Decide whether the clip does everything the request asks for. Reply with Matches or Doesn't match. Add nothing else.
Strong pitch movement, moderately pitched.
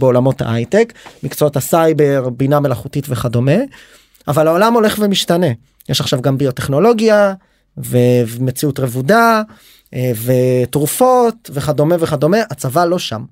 Matches